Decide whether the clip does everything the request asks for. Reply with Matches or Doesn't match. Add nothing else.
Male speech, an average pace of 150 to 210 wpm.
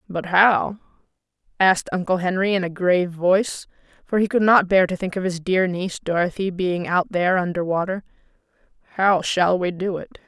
Doesn't match